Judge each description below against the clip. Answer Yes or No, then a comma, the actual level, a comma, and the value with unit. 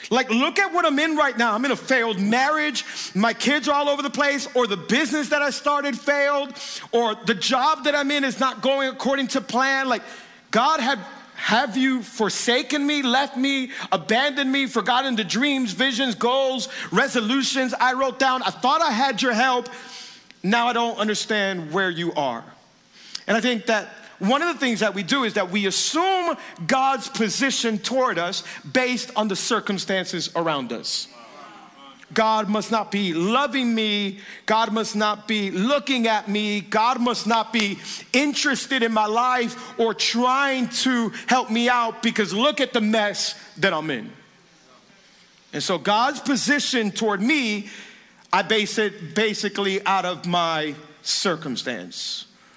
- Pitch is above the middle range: Yes, high, 235 Hz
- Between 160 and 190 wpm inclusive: Yes, average, 165 wpm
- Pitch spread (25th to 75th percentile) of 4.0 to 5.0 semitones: Yes, average, 4.3 semitones